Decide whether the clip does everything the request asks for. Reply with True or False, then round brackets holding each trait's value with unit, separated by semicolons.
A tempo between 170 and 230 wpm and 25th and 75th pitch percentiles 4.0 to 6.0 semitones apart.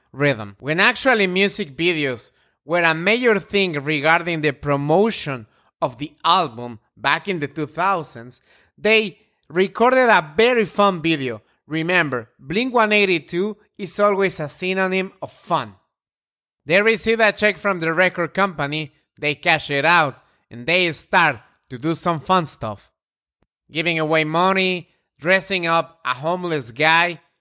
False (135 wpm; 4.8 semitones)